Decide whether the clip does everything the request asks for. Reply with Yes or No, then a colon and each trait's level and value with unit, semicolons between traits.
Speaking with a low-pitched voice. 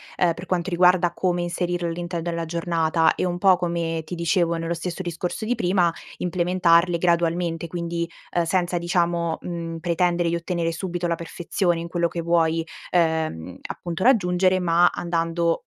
No: medium, 170 Hz